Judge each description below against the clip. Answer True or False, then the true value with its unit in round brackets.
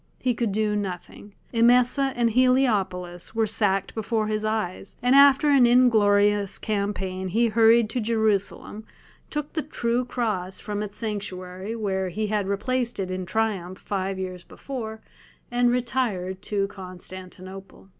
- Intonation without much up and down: False (3.7 semitones)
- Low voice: False (210 Hz)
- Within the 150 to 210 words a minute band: False (140 wpm)